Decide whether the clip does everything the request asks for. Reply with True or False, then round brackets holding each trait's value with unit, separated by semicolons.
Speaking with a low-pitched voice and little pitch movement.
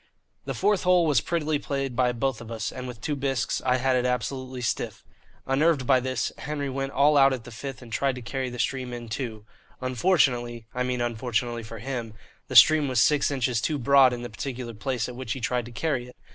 True (125 Hz; 2.3 semitones)